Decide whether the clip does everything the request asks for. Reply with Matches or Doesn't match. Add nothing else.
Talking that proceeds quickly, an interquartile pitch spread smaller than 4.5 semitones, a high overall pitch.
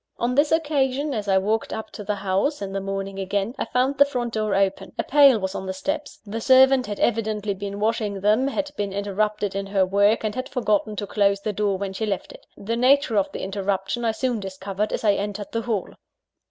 Matches